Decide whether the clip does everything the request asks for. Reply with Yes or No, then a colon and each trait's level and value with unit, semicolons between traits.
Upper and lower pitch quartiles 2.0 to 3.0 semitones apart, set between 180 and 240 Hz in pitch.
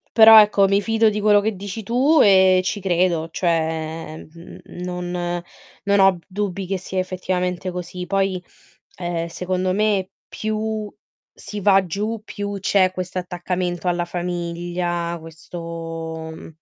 Yes: average, 2.7 semitones; medium, 185 Hz